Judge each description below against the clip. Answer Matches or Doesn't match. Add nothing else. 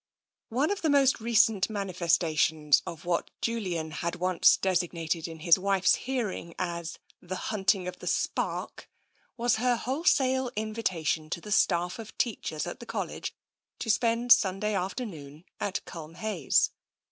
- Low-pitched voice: Doesn't match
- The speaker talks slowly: Doesn't match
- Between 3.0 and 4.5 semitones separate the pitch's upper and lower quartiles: Doesn't match